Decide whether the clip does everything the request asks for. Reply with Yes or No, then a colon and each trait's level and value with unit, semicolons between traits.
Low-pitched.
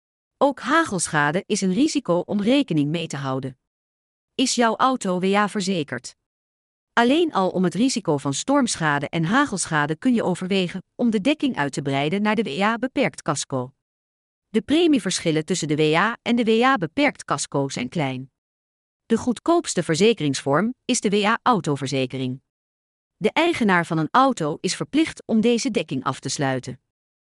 No: medium, 180 Hz